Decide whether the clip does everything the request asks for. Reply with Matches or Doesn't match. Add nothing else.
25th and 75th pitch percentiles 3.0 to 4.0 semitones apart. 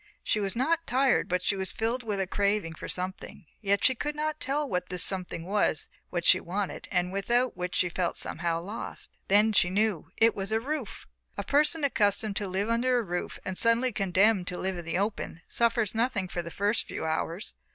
Doesn't match